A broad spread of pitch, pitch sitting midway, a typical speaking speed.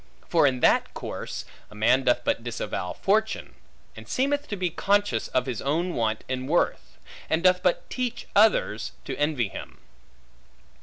Yes: wide, 8.4 semitones; medium, 150 Hz; average, 160 wpm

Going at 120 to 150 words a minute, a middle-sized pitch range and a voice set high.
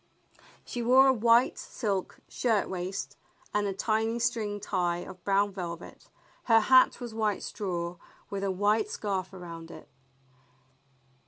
Yes: average, 140 wpm; average, 3.4 semitones; high, 205 Hz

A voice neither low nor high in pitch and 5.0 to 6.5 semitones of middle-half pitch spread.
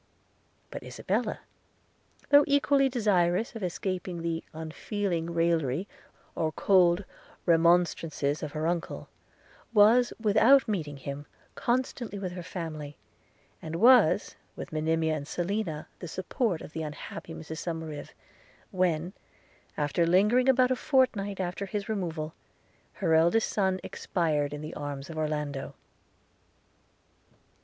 No: medium, 175 Hz; average, 4.6 semitones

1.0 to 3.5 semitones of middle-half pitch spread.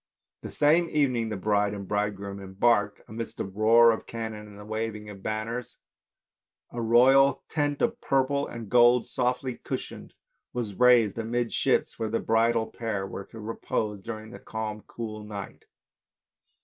Yes: narrow, 2.5 semitones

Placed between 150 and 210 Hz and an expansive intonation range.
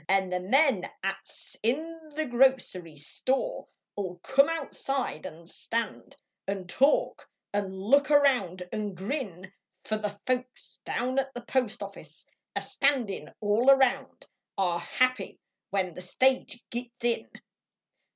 No: high, 235 Hz; wide, 5.9 semitones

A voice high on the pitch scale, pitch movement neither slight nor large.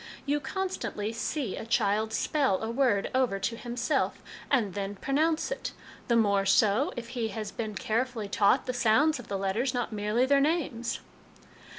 Yes: high, 235 Hz; average, 4.3 semitones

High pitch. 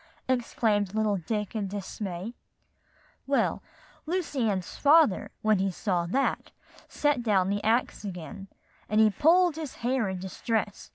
Yes: high, 215 Hz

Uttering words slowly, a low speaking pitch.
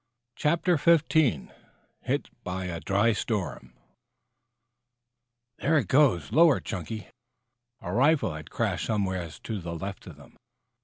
Yes: slow, 120 wpm; low, 100 Hz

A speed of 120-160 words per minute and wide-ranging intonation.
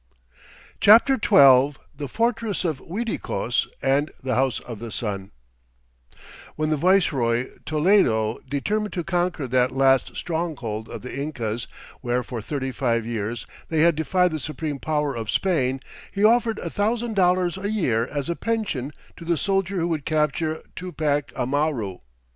Yes: average, 150 wpm; wide, 6.2 semitones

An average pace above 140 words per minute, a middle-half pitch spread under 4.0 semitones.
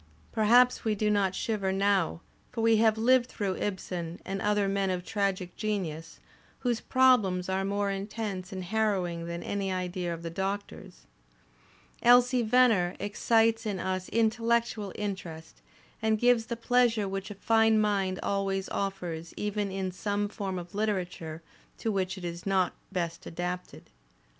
Yes: average, 150 wpm; average, 3.1 semitones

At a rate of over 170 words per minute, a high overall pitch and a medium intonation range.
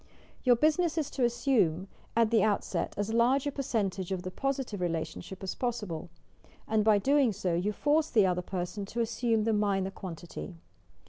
Yes: average, 180 wpm; high, 215 Hz; average, 4.8 semitones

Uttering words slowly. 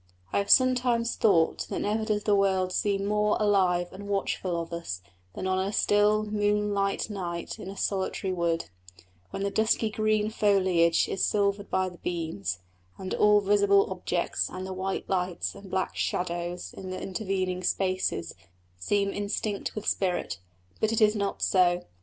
No: average, 165 wpm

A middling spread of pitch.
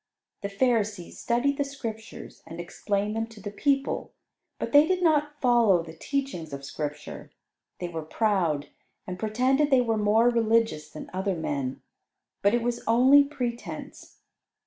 No: wide, 6.3 semitones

